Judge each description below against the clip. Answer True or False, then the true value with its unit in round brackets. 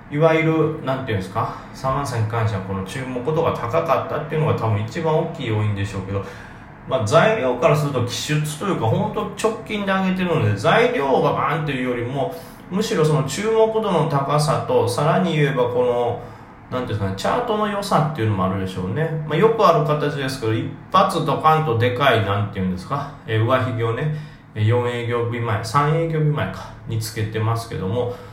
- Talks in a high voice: False (135 Hz)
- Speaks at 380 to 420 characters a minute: True (415 characters per minute)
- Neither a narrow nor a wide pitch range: False (6.0 semitones)